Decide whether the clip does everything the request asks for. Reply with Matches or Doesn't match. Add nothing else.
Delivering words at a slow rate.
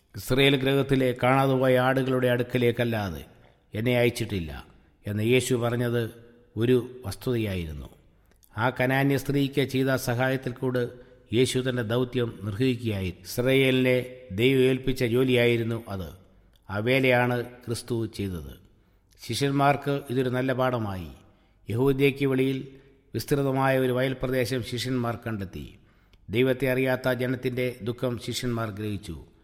Matches